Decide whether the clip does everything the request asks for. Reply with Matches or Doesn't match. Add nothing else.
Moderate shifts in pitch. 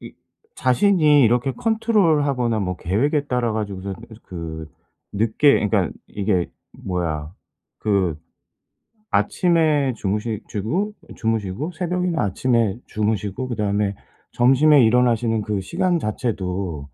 Doesn't match